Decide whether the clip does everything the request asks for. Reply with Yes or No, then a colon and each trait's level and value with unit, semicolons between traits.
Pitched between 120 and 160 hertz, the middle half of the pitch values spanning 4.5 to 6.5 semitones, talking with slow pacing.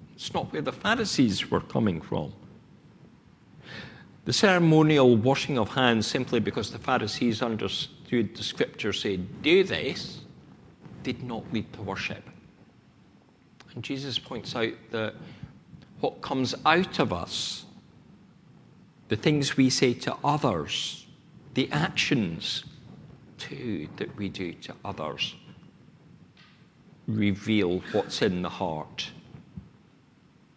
Yes: low, 135 Hz; wide, 5.5 semitones; slow, 110 wpm